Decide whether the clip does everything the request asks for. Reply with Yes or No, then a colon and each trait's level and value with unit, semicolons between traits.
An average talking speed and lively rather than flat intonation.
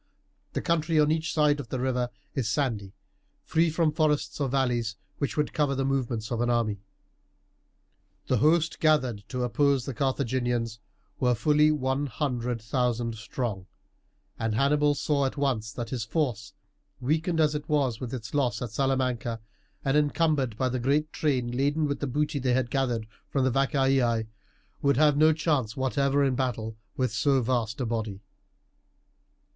No: average, 165 wpm; average, 3.7 semitones